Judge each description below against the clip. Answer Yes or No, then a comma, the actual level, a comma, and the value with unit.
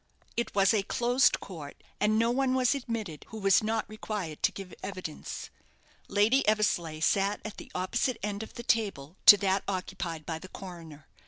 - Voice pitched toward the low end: No, high, 200 Hz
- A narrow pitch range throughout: No, average, 3.6 semitones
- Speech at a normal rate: Yes, average, 175 wpm